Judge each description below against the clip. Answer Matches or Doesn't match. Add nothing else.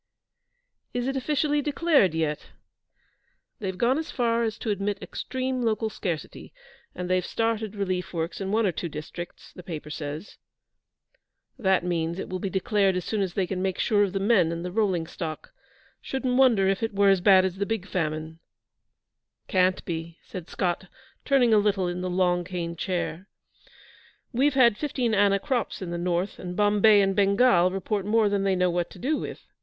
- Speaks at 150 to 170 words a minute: Doesn't match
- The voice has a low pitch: Doesn't match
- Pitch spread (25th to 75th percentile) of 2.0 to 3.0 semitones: Doesn't match